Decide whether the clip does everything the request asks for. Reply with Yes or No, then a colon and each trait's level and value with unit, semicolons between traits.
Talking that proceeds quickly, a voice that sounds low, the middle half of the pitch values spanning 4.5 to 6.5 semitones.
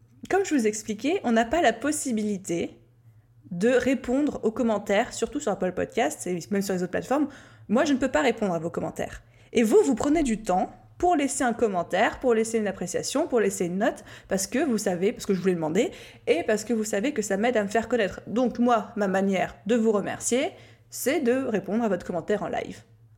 No: fast, 225 wpm; high, 220 Hz; average, 4.8 semitones